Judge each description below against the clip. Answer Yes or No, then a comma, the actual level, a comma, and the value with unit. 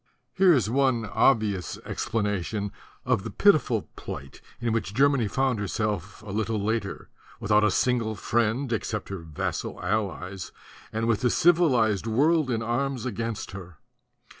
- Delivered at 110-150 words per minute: Yes, average, 140 wpm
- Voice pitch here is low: Yes, low, 110 Hz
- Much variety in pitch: No, average, 3.5 semitones